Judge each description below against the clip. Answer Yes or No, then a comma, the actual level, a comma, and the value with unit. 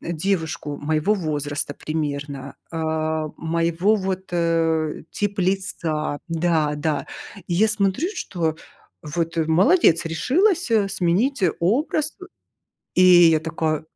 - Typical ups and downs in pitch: Yes, average, 3.8 semitones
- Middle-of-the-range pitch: Yes, medium, 165 Hz